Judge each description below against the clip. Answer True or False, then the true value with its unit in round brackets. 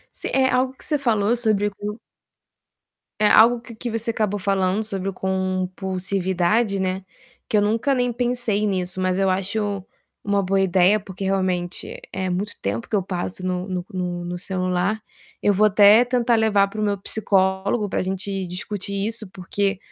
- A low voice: False (200 Hz)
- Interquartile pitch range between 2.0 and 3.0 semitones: True (2.5 semitones)